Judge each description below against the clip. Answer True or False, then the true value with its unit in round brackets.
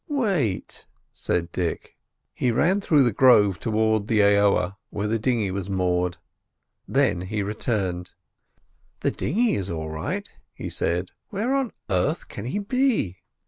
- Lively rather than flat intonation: True (7.0 semitones)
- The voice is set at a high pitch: False (105 Hz)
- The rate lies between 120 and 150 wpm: True (140 wpm)